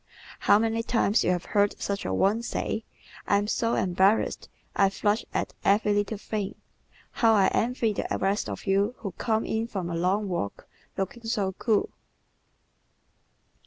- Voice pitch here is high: Yes, high, 205 Hz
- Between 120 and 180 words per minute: Yes, average, 160 wpm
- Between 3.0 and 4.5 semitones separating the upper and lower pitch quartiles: No, narrow, 2.4 semitones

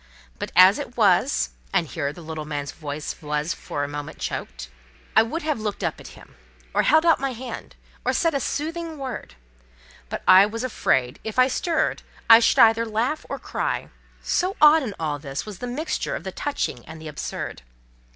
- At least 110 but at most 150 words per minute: No, average, 190 wpm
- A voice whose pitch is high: Yes, high, 220 Hz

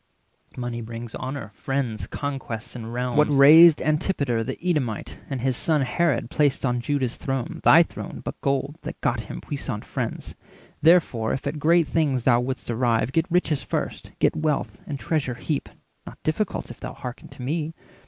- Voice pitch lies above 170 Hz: No, low, 135 Hz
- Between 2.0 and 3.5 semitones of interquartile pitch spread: No, average, 3.9 semitones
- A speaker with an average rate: Yes, average, 175 wpm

